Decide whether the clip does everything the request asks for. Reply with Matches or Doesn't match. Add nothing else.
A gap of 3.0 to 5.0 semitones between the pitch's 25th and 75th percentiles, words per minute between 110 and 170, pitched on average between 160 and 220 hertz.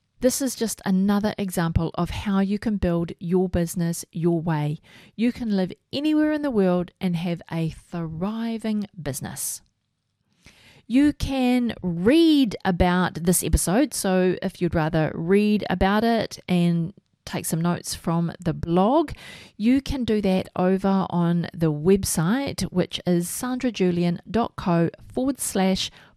Matches